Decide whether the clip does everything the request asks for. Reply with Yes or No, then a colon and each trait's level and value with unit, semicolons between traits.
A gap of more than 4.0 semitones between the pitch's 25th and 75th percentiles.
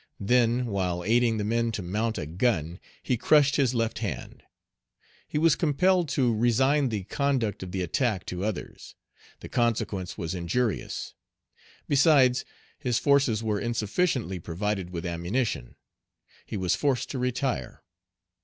Yes: wide, 5.6 semitones